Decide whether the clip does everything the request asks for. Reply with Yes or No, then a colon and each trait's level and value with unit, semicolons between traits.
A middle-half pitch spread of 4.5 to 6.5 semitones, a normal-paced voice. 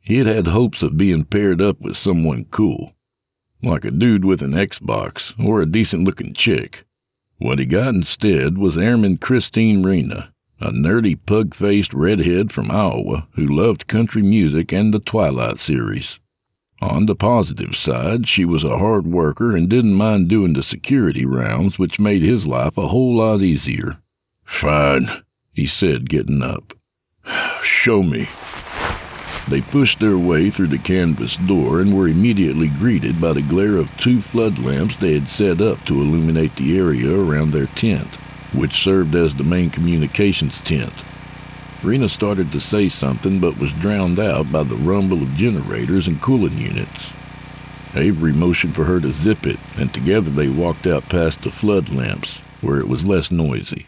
Yes: average, 5.3 semitones; average, 165 wpm